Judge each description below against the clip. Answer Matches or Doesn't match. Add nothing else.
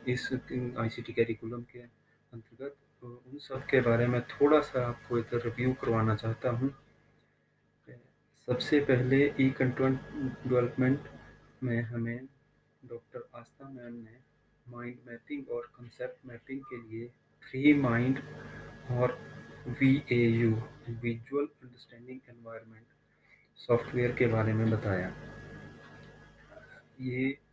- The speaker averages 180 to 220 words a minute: Doesn't match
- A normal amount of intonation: Doesn't match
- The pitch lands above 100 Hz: Matches